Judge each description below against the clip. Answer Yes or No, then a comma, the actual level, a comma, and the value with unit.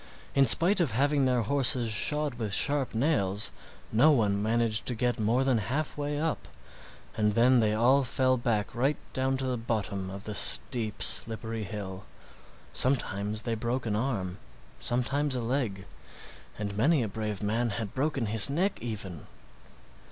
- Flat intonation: No, average, 4.0 semitones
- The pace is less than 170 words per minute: Yes, average, 160 wpm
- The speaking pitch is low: Yes, low, 115 Hz